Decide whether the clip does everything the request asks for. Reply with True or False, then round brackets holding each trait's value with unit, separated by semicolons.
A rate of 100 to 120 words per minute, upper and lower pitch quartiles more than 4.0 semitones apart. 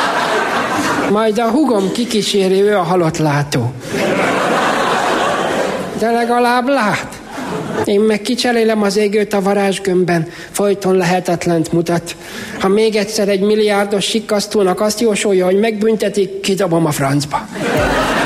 False (110 wpm; 2.9 semitones)